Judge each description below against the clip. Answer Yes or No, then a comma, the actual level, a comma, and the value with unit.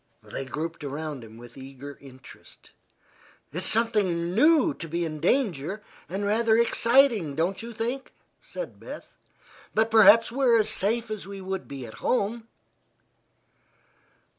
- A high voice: Yes, high, 200 Hz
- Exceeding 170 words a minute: No, average, 140 wpm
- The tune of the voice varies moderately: No, wide, 7.0 semitones